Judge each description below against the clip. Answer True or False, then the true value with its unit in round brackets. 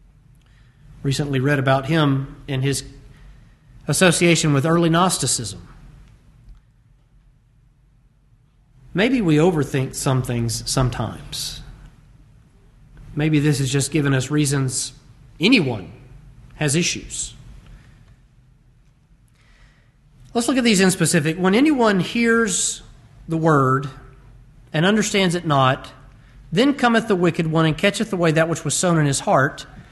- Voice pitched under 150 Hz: True (140 Hz)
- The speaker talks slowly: True (110 wpm)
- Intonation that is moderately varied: True (3.7 semitones)